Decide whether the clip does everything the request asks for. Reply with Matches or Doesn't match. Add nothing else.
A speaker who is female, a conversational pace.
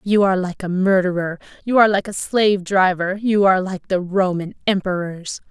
Matches